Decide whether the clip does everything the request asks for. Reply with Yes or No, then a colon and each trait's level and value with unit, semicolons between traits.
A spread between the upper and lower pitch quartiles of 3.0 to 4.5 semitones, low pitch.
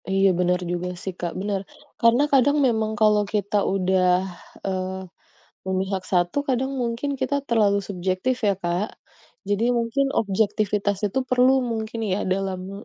No: average, 4.1 semitones; high, 205 Hz